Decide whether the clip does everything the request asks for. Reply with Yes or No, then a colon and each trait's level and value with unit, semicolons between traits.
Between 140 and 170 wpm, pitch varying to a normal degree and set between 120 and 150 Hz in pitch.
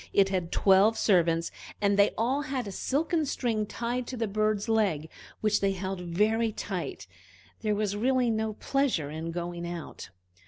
No: average, 165 wpm; average, 4.1 semitones; high, 210 Hz